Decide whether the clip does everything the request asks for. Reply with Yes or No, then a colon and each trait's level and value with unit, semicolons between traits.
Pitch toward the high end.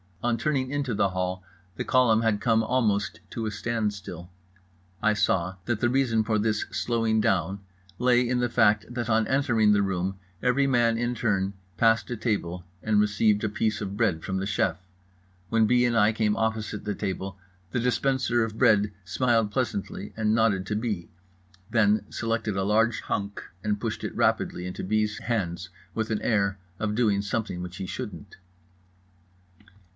No: low, 110 Hz